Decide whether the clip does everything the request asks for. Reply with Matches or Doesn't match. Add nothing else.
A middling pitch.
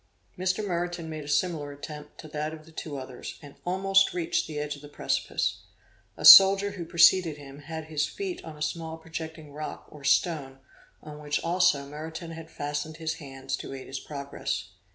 Matches